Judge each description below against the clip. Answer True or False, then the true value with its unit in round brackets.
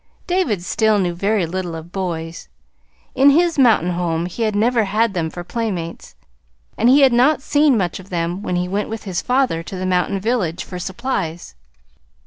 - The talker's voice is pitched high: True (195 Hz)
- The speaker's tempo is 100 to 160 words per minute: False (185 wpm)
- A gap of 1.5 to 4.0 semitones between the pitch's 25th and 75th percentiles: False (5.2 semitones)